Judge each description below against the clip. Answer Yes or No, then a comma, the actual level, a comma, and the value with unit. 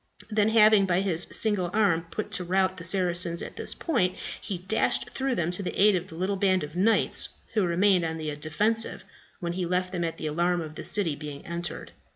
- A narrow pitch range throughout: No, average, 3.0 semitones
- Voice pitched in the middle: Yes, medium, 180 Hz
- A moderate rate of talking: No, fast, 220 wpm